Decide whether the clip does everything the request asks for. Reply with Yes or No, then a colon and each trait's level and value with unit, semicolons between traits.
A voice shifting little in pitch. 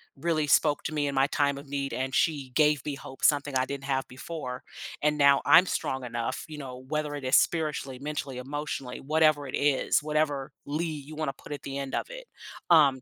Yes: narrow, 2.2 semitones